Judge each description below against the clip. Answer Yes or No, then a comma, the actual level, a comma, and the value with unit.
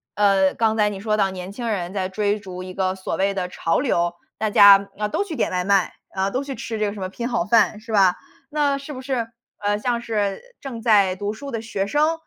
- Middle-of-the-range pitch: No, high, 205 Hz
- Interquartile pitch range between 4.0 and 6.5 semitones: No, average, 3.3 semitones